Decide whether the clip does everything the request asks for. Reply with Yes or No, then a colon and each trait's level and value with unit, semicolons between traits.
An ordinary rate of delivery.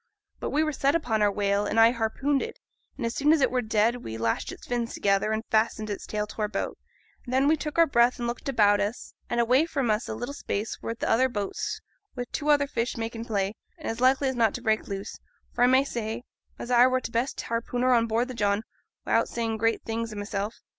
No: fast, 240 wpm